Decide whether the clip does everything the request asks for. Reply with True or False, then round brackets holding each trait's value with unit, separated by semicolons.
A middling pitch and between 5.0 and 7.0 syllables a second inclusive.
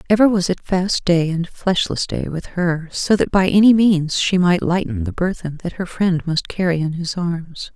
False (175 Hz; 4.5 syllables/s)